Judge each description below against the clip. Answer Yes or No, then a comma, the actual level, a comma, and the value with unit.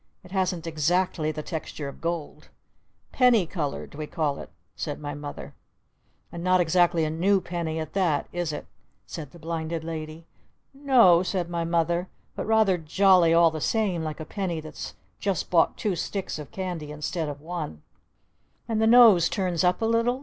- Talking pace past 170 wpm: Yes, average, 180 wpm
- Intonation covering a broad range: No, average, 3.1 semitones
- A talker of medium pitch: Yes, medium, 170 Hz